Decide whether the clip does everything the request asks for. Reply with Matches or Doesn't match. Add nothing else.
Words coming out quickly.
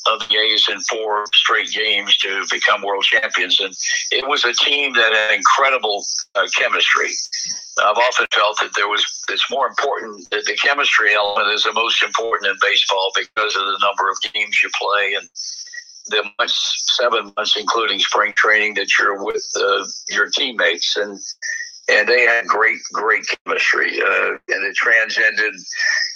Doesn't match